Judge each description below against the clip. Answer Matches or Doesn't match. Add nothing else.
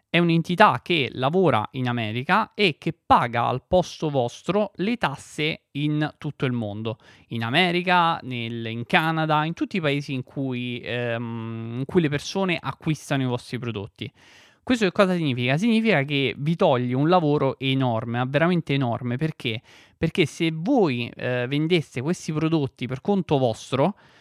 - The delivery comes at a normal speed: Matches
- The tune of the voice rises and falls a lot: Matches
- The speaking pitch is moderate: Matches